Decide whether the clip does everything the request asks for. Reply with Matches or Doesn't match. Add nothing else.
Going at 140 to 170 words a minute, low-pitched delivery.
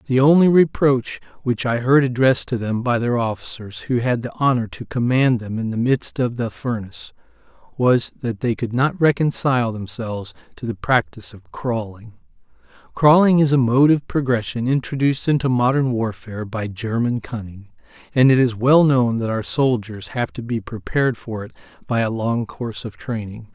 Doesn't match